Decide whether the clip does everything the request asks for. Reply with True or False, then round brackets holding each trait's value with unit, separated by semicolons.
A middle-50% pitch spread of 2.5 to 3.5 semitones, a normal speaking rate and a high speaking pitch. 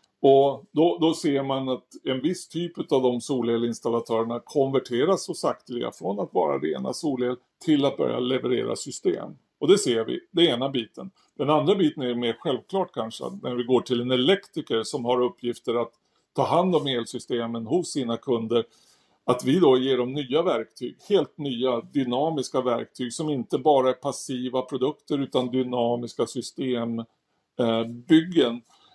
False (2.8 semitones; 160 wpm; 130 Hz)